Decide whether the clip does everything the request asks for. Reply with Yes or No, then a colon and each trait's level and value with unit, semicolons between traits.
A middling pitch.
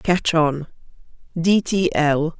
Yes: medium, 170 Hz